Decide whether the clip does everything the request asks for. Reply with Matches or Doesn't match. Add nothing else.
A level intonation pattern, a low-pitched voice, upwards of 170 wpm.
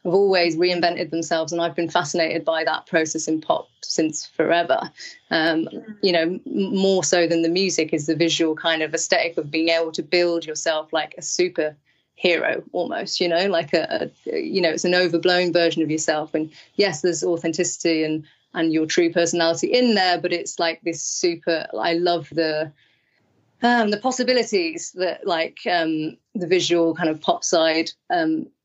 Doesn't match